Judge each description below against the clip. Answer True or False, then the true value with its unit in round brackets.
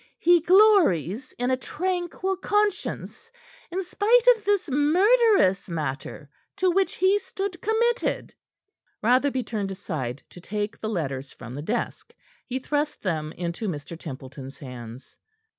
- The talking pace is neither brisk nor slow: False (130 wpm)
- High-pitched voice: True (255 Hz)